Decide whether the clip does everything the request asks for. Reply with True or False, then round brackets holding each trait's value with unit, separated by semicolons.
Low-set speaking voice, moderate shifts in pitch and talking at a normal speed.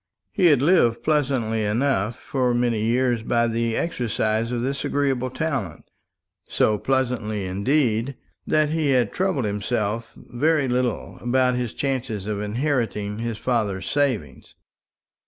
False (120 Hz; 3.8 semitones; 130 wpm)